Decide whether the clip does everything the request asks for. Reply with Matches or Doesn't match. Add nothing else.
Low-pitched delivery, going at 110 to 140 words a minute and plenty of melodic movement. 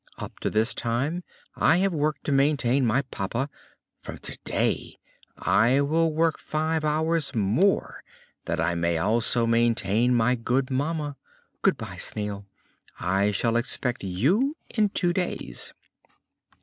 Matches